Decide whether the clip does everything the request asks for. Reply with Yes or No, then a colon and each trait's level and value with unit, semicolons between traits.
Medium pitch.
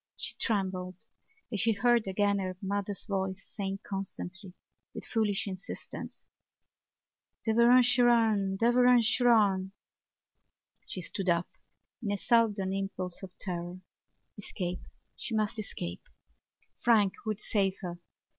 No: high, 200 Hz